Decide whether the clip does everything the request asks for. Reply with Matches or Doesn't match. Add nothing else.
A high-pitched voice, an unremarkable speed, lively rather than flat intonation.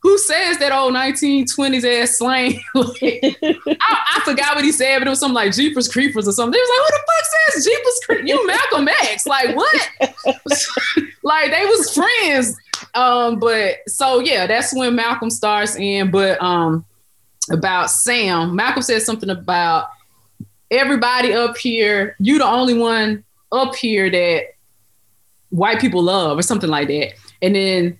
Matches